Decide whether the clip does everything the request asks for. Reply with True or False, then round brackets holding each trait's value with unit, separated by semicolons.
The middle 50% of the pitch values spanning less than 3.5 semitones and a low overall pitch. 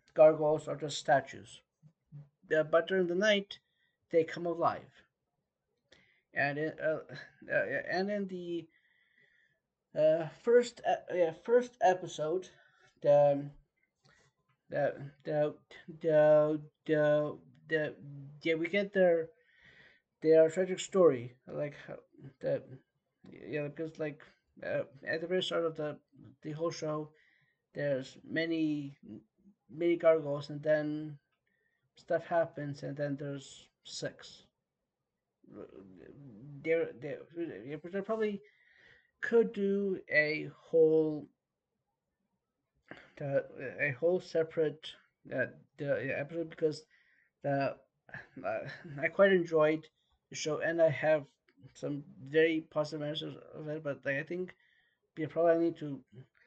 False (3.1 semitones; 160 Hz)